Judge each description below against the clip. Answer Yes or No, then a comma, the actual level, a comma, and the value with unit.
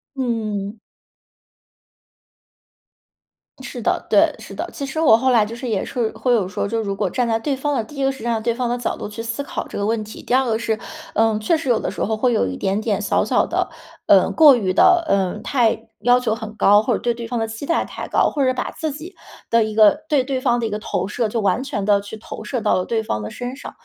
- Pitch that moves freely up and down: No, average, 3.2 semitones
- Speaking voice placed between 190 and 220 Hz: No, high, 230 Hz